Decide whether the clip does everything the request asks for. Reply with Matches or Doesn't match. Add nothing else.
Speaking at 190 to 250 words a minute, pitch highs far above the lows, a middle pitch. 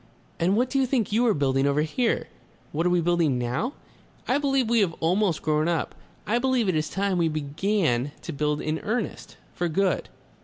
Matches